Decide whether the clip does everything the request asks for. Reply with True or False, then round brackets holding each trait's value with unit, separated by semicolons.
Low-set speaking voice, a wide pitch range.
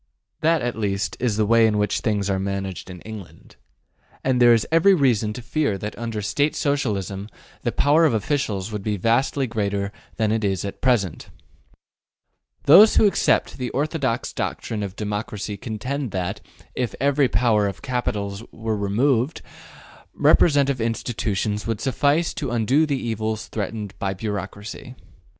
False (110 Hz; 4.4 semitones)